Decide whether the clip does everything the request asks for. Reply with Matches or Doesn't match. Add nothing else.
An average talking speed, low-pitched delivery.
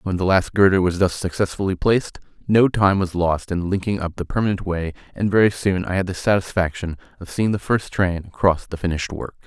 Doesn't match